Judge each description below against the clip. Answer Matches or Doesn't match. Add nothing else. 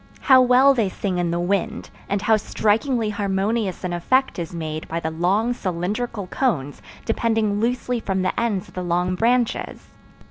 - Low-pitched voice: Doesn't match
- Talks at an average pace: Matches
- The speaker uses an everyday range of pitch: Matches